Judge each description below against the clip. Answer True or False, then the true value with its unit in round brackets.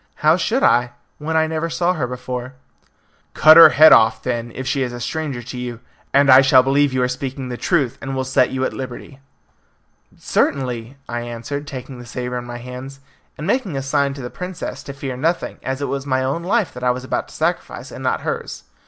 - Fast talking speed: True (225 wpm)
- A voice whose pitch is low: True (130 Hz)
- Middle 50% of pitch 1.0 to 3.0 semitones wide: True (2.7 semitones)